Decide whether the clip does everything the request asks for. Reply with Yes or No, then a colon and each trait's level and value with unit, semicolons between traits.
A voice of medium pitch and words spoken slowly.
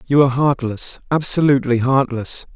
No: low, 130 Hz; slow, 95 wpm